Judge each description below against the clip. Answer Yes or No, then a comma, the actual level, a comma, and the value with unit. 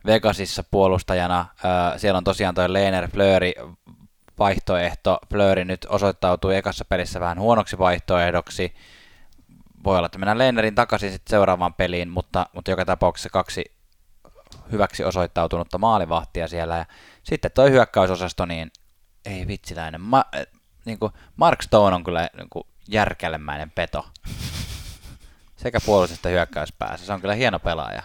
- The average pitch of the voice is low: Yes, very low, 90 Hz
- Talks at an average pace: Yes, average, 130 wpm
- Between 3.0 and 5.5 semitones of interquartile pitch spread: No, narrow, 2.5 semitones